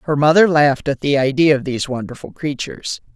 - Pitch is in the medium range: Yes, medium, 145 Hz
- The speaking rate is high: No, average, 190 wpm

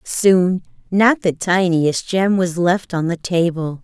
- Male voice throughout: No, female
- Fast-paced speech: No, average, 155 wpm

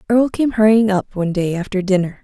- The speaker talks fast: Yes, fast, 215 wpm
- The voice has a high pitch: Yes, high, 200 Hz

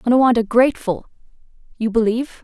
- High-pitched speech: Yes, high, 235 Hz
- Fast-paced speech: No, slow, 100 wpm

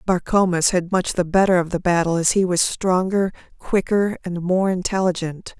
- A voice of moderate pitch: Yes, medium, 180 Hz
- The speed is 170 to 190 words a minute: Yes, average, 180 wpm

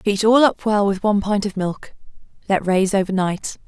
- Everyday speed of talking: No, fast, 210 wpm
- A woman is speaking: Yes, female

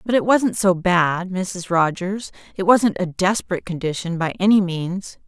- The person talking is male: No, female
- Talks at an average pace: Yes, average, 170 wpm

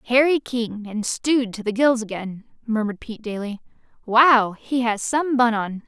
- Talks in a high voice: Yes, high, 230 Hz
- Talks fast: No, average, 175 wpm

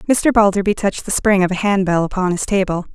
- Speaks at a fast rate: Yes, fast, 225 wpm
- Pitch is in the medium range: No, high, 195 Hz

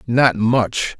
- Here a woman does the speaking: No, male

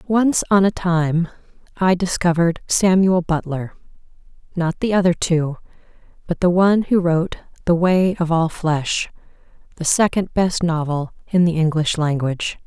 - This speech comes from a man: No, female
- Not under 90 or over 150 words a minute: Yes, average, 140 wpm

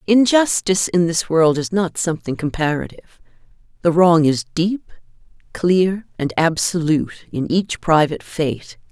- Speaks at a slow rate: Yes, slow, 130 wpm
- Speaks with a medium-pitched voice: Yes, medium, 165 Hz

